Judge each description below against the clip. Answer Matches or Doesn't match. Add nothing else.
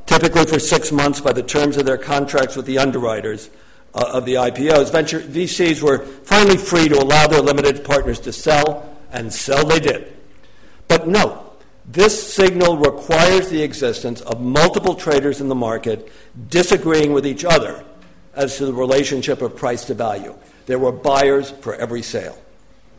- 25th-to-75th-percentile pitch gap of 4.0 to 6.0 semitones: Doesn't match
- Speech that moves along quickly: Doesn't match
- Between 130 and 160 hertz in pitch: Matches